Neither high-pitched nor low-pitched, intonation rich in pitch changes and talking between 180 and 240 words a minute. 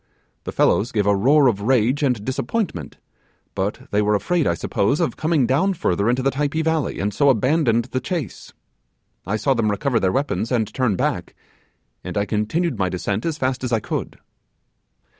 No: low, 125 Hz; wide, 5.7 semitones; average, 185 wpm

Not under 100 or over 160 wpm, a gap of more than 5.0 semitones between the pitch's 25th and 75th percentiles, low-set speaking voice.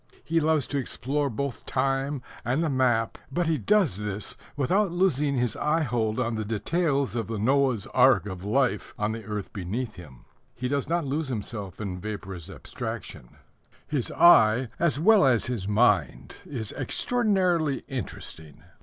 Yes: average, 155 wpm; wide, 5.6 semitones; low, 125 Hz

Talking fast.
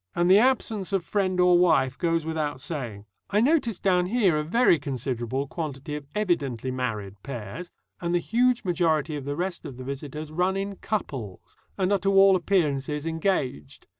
No: average, 175 wpm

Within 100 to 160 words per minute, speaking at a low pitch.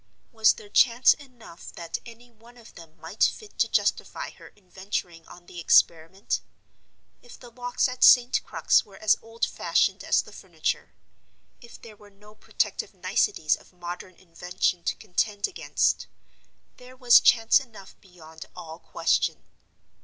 No: average, 145 wpm; high, 210 Hz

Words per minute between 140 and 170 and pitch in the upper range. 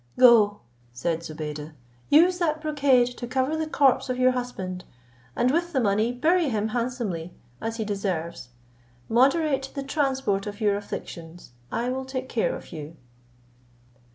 Yes: average, 150 wpm; high, 245 Hz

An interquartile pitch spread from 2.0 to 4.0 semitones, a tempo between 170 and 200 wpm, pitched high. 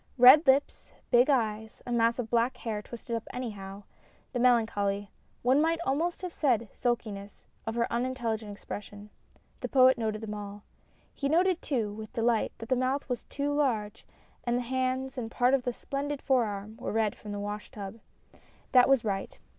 Yes: average, 3.5 semitones; average, 185 wpm; high, 235 Hz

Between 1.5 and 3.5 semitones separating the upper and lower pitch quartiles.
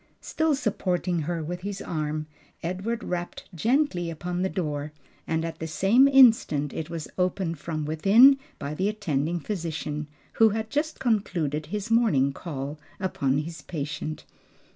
No: wide, 5.5 semitones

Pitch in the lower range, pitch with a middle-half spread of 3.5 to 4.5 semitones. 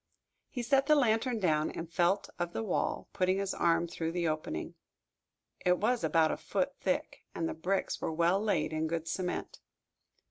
No: medium, 175 Hz; average, 3.9 semitones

